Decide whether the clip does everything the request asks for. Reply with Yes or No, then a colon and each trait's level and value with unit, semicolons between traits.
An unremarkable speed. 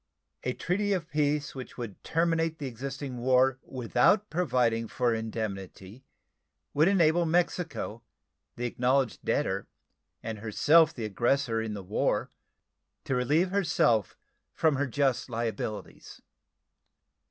No: slow, 120 wpm